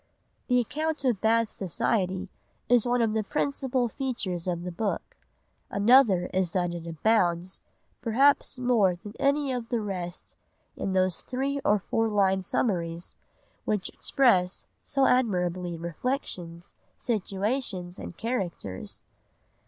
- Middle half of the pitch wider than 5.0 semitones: Yes, wide, 5.6 semitones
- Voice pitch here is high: Yes, high, 205 Hz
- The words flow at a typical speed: No, slow, 125 wpm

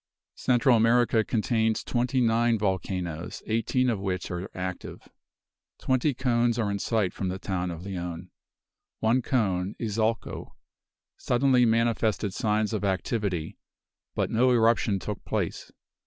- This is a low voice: Yes, low, 110 Hz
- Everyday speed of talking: No, slow, 125 wpm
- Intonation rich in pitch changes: No, average, 3.8 semitones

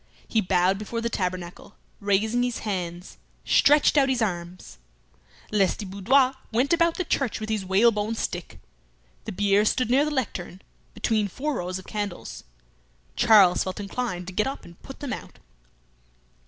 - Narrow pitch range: No, average, 4.8 semitones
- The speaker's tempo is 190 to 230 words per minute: No, average, 155 wpm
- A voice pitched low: No, high, 210 Hz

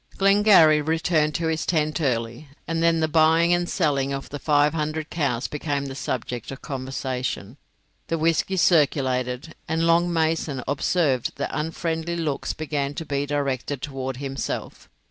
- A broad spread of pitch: No, average, 3.1 semitones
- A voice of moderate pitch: Yes, medium, 150 Hz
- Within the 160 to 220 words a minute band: No, average, 150 wpm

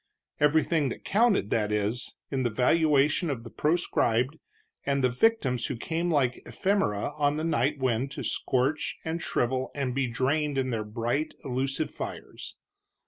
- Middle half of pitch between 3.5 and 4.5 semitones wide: Yes, average, 4.0 semitones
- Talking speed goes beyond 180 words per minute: No, average, 155 wpm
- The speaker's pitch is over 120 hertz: Yes, low, 135 Hz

